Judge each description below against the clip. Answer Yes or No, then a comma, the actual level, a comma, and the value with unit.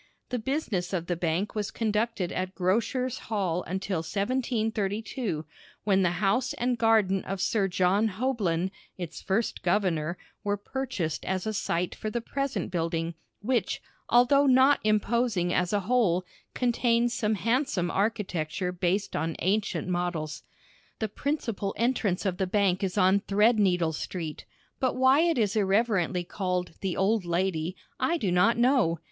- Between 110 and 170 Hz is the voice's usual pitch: No, high, 200 Hz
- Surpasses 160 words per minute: No, average, 145 wpm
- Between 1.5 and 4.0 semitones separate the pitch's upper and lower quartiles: No, average, 4.4 semitones